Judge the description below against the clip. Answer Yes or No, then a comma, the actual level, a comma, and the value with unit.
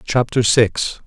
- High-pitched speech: No, low, 110 Hz